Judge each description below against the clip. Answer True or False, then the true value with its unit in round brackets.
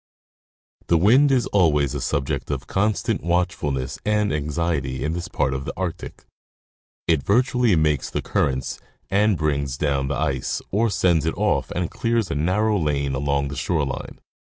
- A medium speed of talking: True (165 wpm)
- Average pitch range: False (5.8 semitones)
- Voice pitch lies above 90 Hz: False (80 Hz)